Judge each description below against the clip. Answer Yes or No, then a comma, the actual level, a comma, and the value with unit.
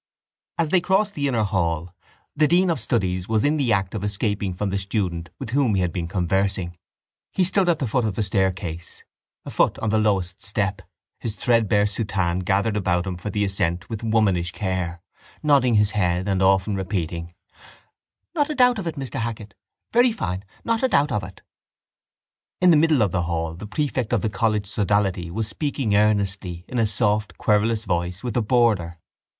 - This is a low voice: Yes, low, 105 Hz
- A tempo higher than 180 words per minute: Yes, average, 190 wpm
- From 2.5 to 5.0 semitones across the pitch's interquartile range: Yes, average, 4.2 semitones